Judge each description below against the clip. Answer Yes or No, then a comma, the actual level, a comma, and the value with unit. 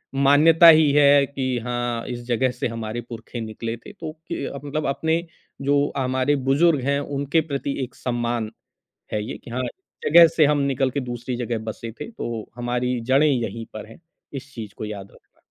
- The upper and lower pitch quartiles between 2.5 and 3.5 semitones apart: Yes, average, 3.2 semitones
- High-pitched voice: No, low, 130 Hz